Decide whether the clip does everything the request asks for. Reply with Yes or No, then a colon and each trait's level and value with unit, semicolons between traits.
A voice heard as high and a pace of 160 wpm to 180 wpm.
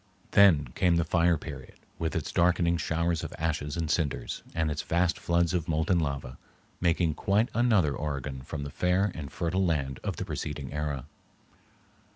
No: very low, 80 Hz; average, 170 wpm